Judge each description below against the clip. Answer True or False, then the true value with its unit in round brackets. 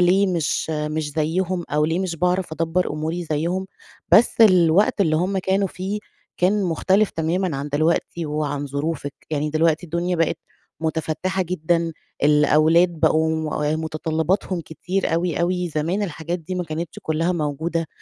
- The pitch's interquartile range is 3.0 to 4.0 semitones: False (2.6 semitones)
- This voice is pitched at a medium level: True (165 Hz)